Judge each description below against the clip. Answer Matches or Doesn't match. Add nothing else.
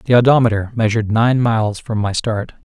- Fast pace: Doesn't match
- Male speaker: Matches